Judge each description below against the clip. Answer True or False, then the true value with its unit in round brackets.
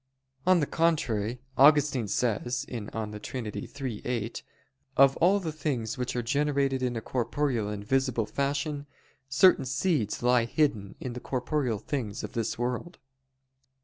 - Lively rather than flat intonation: False (4.0 semitones)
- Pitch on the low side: True (125 Hz)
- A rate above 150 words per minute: False (145 wpm)